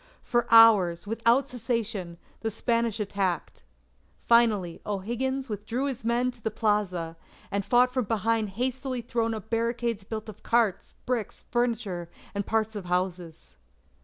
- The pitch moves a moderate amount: Yes, average, 3.1 semitones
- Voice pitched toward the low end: No, high, 225 Hz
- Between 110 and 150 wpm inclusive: Yes, slow, 135 wpm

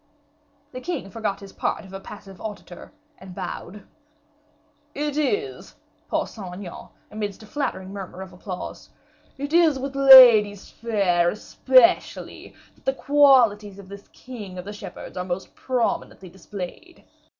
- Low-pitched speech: No, high, 210 Hz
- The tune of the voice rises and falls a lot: Yes, wide, 5.7 semitones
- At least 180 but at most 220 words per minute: No, average, 140 wpm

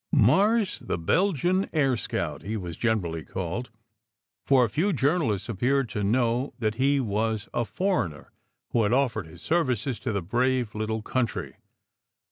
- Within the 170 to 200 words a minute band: No, average, 155 wpm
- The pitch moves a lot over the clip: No, average, 4.7 semitones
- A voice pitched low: Yes, low, 120 Hz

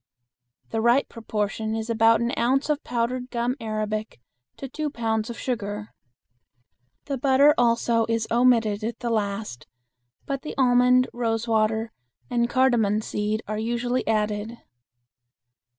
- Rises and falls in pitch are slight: Yes, narrow, 2.2 semitones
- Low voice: No, high, 230 Hz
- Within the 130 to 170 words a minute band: Yes, slow, 135 wpm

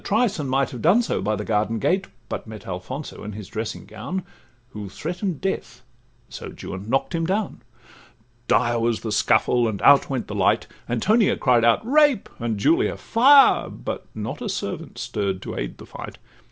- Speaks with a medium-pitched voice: No, low, 120 Hz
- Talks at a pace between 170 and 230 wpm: Yes, average, 180 wpm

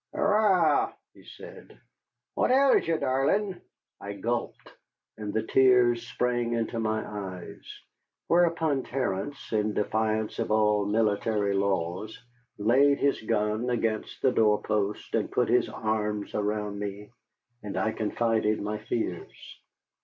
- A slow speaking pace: Yes, slow, 125 wpm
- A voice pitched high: No, low, 110 Hz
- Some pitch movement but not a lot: Yes, average, 3.3 semitones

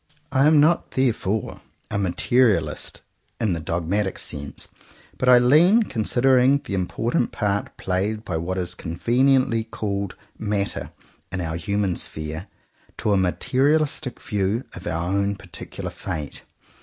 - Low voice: Yes, low, 100 Hz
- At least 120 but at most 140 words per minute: Yes, slow, 135 wpm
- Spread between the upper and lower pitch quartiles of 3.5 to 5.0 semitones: No, wide, 5.6 semitones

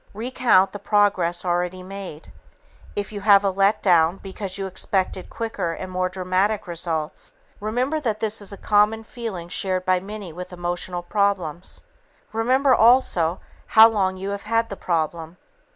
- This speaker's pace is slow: No, average, 155 wpm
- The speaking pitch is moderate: No, high, 195 Hz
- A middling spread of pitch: Yes, average, 3.1 semitones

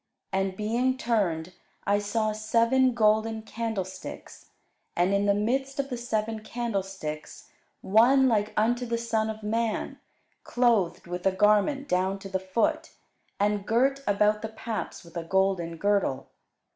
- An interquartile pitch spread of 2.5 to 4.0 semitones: Yes, average, 3.2 semitones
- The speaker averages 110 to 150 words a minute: Yes, average, 145 wpm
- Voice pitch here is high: Yes, high, 215 Hz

